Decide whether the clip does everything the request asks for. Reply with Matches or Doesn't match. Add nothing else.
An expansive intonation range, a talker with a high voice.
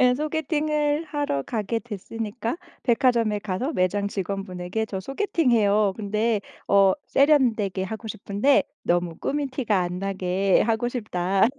Doesn't match